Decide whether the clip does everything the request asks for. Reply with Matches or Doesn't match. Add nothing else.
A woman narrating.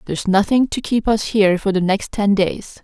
Matches